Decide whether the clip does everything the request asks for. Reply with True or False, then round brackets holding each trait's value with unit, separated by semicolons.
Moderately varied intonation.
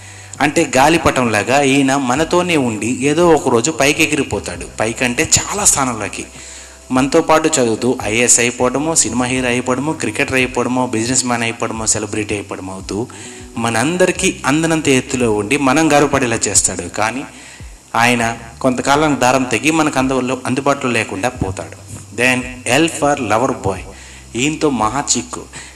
True (4.3 semitones)